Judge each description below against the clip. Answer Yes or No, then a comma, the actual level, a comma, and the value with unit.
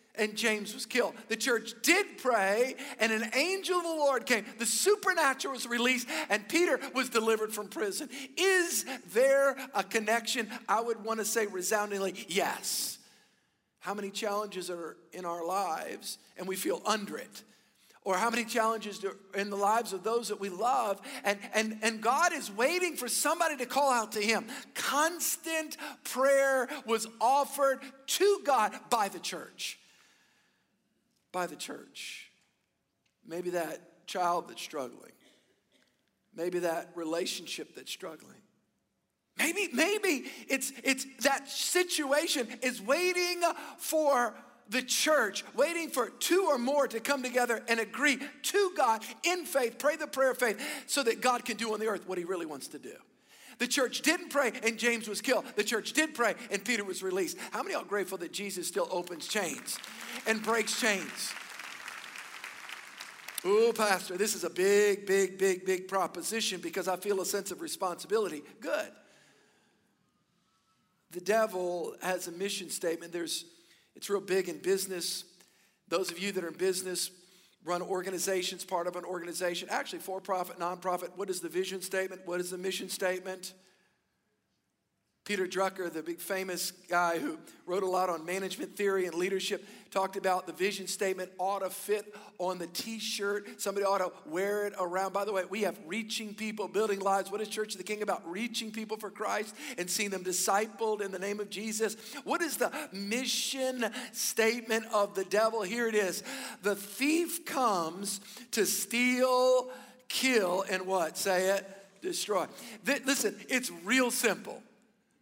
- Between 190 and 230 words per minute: No, average, 165 wpm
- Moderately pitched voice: No, high, 215 Hz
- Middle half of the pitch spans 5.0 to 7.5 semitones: Yes, average, 5.3 semitones